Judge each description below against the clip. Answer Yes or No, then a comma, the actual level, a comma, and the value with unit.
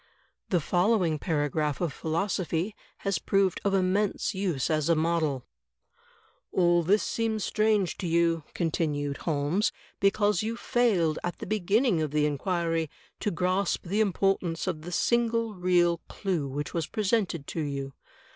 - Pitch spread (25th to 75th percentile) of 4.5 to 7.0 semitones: No, average, 4.1 semitones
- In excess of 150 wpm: No, average, 145 wpm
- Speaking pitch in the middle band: Yes, medium, 175 Hz